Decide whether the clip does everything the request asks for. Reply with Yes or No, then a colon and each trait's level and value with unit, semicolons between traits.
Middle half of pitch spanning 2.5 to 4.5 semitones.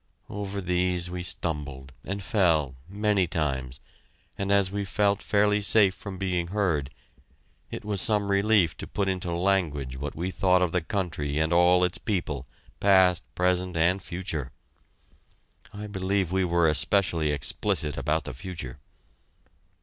Yes: average, 3.7 semitones